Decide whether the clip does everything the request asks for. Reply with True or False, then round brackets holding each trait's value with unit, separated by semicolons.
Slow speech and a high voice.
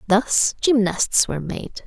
True (130 wpm; 215 Hz)